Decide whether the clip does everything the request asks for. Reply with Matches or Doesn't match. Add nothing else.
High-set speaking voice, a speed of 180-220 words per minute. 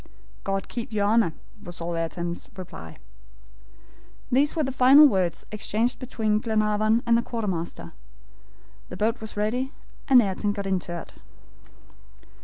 Doesn't match